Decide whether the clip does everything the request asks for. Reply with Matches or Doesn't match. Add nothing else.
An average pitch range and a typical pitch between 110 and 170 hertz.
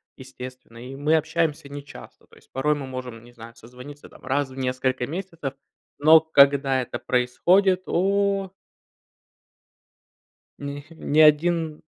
Matches